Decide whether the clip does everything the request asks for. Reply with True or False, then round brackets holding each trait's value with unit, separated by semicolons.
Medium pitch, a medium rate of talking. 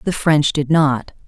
True (150 Hz; 190 wpm)